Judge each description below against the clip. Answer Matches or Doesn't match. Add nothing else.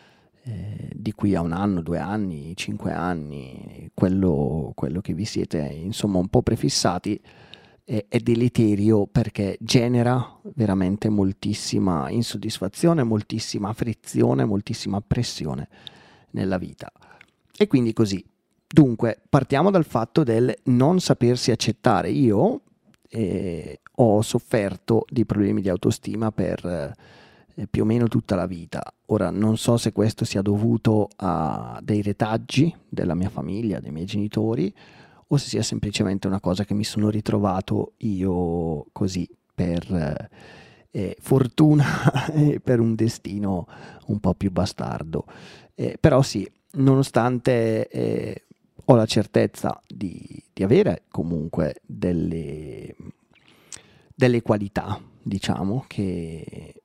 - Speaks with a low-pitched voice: Matches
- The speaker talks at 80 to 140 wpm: Matches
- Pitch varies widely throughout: Doesn't match